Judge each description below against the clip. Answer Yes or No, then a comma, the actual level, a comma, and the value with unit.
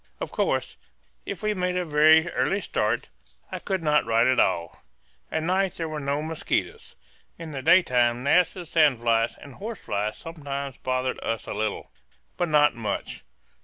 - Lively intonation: Yes, wide, 5.7 semitones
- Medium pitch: Yes, medium, 150 Hz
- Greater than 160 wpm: Yes, average, 170 wpm